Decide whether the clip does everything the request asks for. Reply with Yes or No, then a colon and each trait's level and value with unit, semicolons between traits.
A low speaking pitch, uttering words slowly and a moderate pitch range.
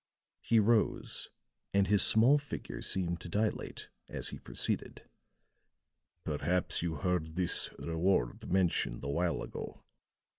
Yes: very low, 90 Hz; slow, 120 wpm; average, 3.7 semitones